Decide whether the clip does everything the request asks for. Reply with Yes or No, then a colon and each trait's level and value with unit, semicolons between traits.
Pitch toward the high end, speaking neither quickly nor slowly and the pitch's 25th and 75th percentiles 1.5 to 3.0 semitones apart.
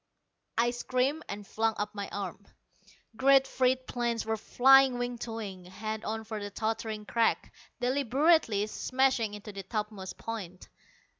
No: high, 225 Hz; average, 145 wpm; average, 3.4 semitones